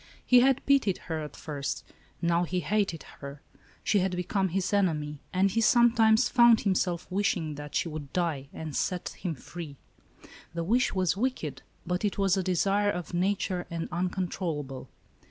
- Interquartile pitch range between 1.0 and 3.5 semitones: No, average, 4.1 semitones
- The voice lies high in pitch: No, medium, 180 Hz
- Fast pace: No, average, 170 wpm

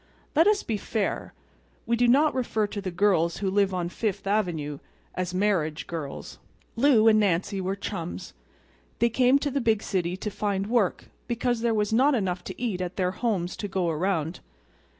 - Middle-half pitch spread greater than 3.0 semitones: Yes, average, 4.2 semitones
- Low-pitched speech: No, high, 200 Hz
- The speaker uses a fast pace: No, average, 185 wpm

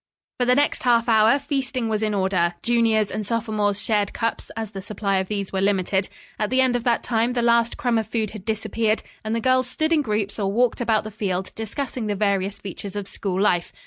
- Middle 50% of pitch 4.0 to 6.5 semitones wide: No, average, 2.8 semitones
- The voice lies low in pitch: No, high, 220 Hz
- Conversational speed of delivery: No, fast, 225 wpm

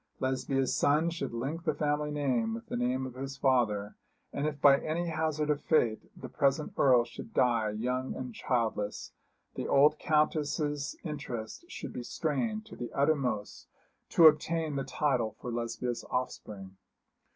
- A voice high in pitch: No, low, 135 Hz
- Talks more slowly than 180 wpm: Yes, average, 155 wpm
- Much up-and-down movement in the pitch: No, average, 4.0 semitones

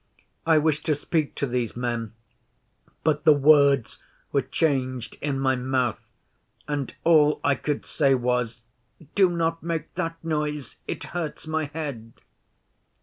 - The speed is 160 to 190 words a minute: No, average, 140 wpm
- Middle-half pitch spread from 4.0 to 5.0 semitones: No, average, 3.6 semitones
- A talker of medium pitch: Yes, medium, 145 Hz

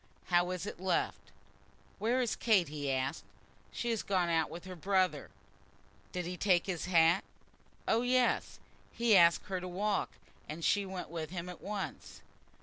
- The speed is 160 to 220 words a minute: Yes, average, 165 wpm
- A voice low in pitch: No, medium, 185 Hz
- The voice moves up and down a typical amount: Yes, average, 3.1 semitones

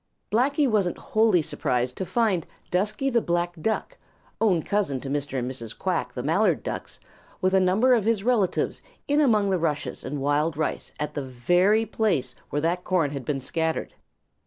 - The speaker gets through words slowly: No, average, 180 wpm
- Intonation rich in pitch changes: Yes, wide, 6.7 semitones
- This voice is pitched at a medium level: Yes, medium, 180 Hz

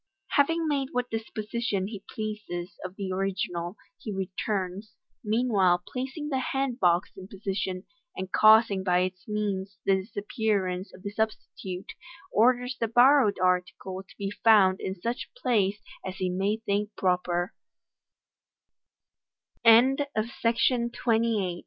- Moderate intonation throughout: Yes, average, 3.3 semitones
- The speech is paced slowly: Yes, slow, 115 wpm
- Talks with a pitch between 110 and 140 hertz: No, high, 200 Hz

